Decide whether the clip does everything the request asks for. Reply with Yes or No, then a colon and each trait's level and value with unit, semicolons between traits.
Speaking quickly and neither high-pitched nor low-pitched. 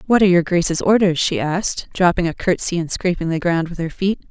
Yes: fast, 235 wpm; medium, 175 Hz